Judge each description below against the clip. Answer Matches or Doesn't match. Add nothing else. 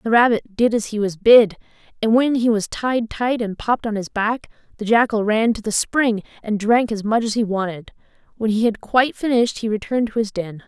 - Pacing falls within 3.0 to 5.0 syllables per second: Doesn't match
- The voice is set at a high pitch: Matches